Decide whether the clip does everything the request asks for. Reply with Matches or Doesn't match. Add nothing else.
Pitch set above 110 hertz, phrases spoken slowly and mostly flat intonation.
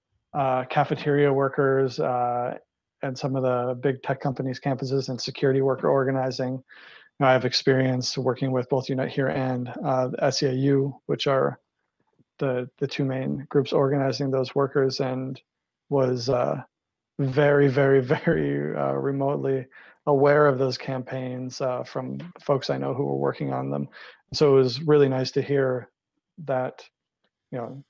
Doesn't match